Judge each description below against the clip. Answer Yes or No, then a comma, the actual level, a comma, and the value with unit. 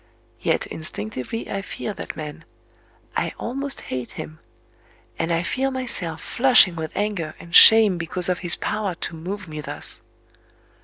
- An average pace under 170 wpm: Yes, average, 145 wpm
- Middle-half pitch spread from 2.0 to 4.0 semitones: No, average, 5.1 semitones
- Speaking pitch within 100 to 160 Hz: No, medium, 175 Hz